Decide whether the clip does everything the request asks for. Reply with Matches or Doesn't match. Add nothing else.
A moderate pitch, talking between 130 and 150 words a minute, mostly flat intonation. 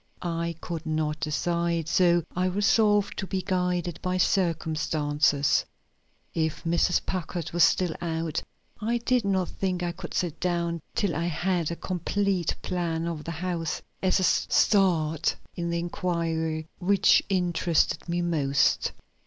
Matches